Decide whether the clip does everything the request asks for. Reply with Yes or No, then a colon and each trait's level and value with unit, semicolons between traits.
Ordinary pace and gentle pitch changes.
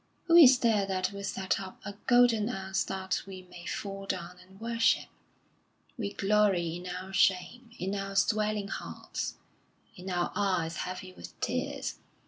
Yes: average, 155 wpm; narrow, 2.3 semitones